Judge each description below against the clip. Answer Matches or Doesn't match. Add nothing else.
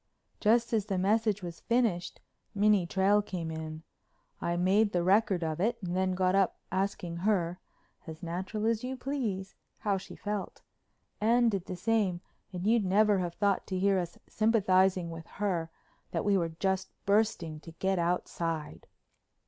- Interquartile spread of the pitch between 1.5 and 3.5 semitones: Matches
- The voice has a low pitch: Doesn't match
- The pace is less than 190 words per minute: Matches